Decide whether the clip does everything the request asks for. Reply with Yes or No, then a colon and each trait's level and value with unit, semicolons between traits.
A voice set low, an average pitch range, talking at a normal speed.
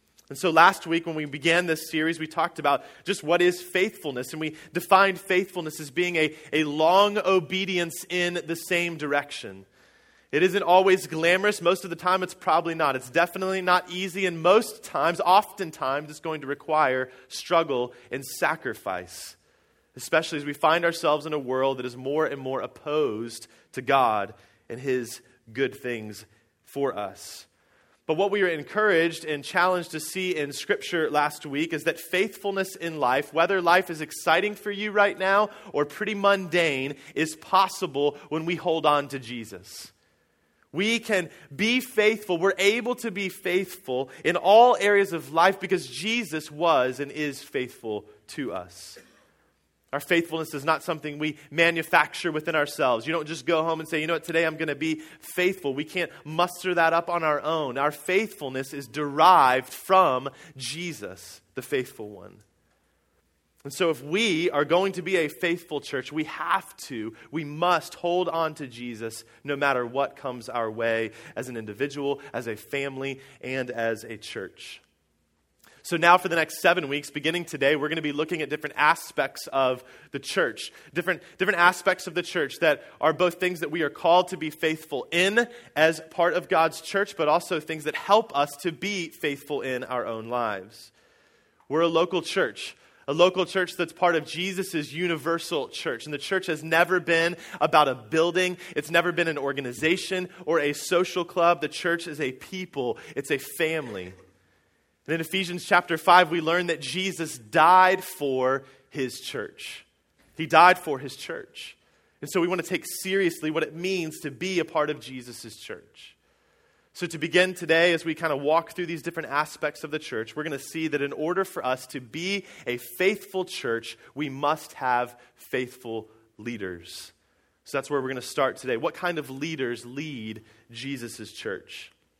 No: medium, 160 Hz; average, 4.4 semitones; average, 180 wpm